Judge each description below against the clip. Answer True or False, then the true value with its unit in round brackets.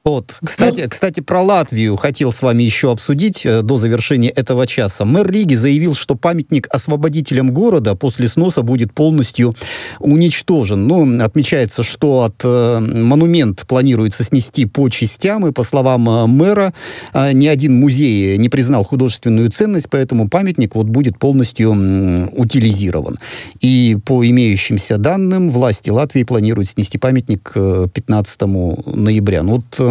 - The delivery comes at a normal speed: True (130 wpm)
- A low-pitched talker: True (125 Hz)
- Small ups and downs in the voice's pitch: False (4.7 semitones)